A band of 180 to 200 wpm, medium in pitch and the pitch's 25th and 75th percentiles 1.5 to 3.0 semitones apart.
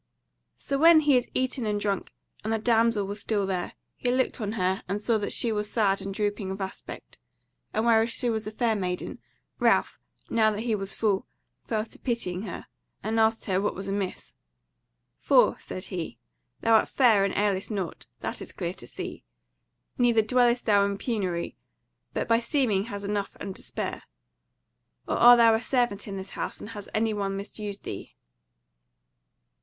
No: average, 185 wpm; high, 210 Hz; average, 2.7 semitones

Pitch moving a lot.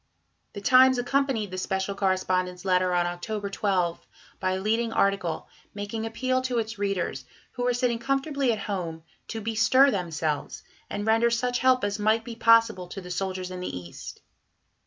No: average, 4.3 semitones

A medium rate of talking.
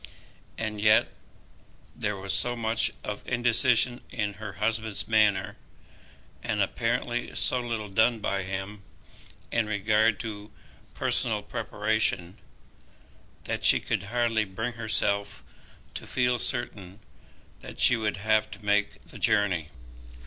No: slow, 120 wpm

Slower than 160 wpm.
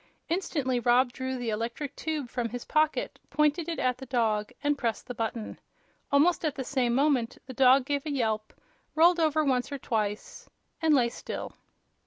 No: average, 180 wpm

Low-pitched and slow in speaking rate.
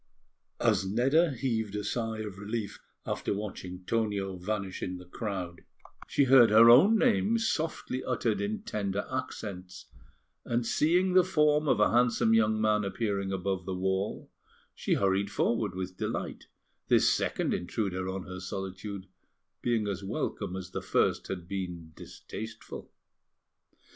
No: low, 105 Hz; average, 145 wpm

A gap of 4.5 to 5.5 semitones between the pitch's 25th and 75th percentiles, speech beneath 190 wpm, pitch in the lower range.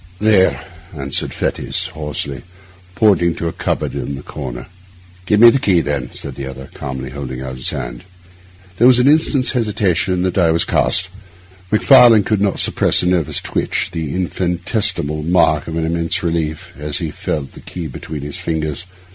Yes: average, 5.2 semitones; average, 175 wpm; very low, 85 Hz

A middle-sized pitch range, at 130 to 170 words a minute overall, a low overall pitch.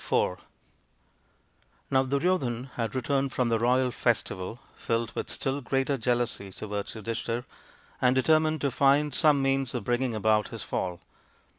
Yes: average, 3.0 semitones; average, 140 wpm; low, 125 Hz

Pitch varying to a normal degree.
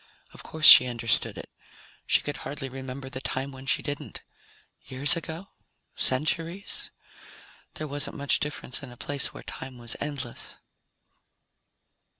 No: narrow, 2.3 semitones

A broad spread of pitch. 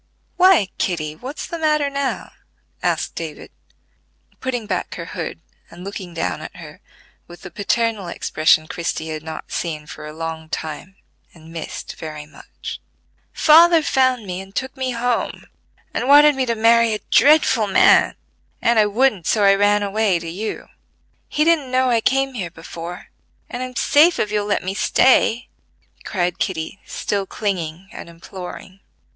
Yes: wide, 7.0 semitones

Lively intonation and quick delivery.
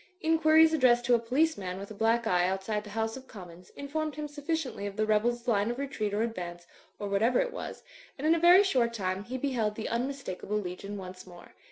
Yes: wide, 5.7 semitones; fast, 220 wpm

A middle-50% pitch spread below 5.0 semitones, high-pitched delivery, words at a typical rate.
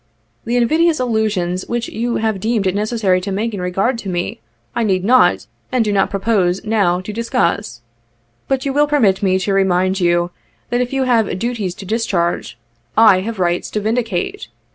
Yes: average, 4.0 semitones; high, 210 Hz; average, 185 wpm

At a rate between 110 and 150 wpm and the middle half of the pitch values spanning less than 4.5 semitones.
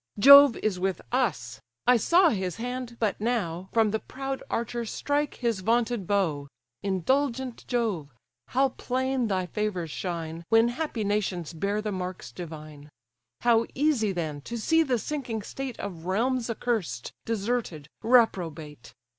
No: average, 140 wpm; wide, 5.5 semitones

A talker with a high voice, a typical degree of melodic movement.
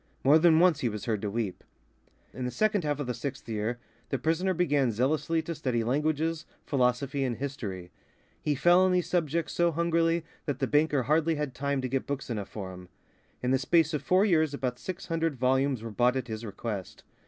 No: medium, 140 Hz; average, 4.9 semitones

